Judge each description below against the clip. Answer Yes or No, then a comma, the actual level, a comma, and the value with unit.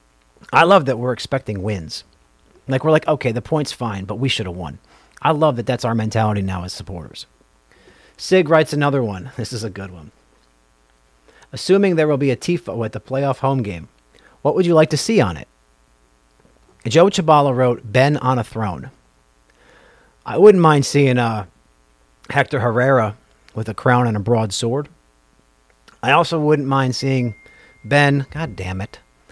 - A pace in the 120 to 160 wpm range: No, average, 175 wpm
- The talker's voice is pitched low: Yes, low, 115 Hz